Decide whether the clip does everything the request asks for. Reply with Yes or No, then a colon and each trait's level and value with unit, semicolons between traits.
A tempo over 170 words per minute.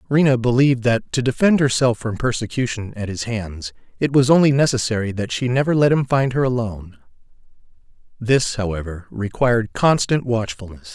No: average, 155 wpm